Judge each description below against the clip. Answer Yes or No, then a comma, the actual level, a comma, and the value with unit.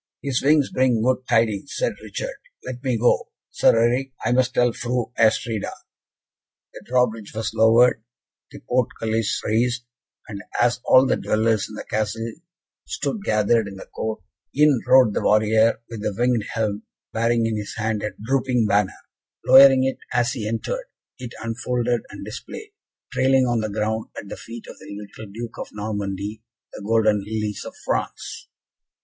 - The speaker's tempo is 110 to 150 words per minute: No, average, 165 wpm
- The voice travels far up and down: No, narrow, 2.6 semitones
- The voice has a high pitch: No, low, 115 Hz